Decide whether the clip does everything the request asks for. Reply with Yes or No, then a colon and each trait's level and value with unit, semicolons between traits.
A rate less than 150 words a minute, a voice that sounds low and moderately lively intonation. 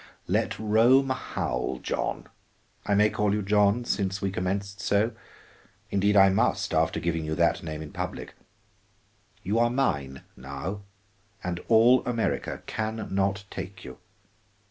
Yes: average, 140 wpm; low, 100 Hz; average, 3.7 semitones